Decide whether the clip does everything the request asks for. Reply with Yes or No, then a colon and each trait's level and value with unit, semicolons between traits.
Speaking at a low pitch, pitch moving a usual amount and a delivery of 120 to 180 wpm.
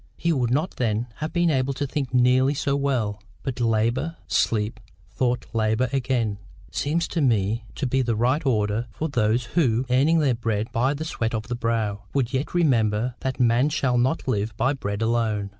No: low, 125 Hz; average, 3.6 semitones; average, 190 wpm